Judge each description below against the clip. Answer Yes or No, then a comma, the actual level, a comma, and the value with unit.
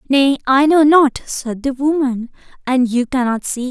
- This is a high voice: Yes, very high, 265 Hz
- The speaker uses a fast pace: No, average, 180 wpm